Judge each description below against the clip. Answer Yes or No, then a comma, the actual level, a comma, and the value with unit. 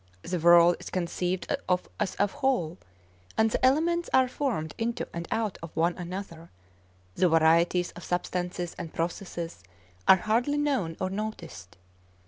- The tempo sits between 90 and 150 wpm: Yes, average, 145 wpm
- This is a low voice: No, medium, 180 Hz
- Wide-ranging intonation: No, average, 4.6 semitones